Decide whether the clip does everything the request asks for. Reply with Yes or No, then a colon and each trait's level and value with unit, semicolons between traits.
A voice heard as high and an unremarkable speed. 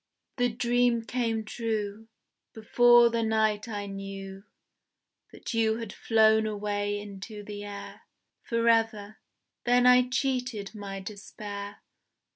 No: high, 220 Hz; slow, 110 wpm